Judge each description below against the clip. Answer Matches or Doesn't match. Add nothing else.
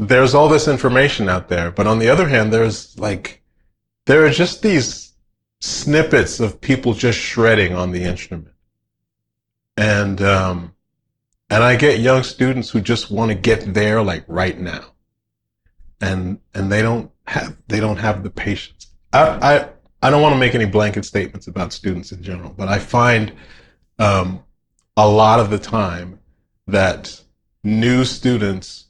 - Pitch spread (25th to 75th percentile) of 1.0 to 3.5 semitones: Doesn't match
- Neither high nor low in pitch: Doesn't match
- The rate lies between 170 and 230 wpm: Doesn't match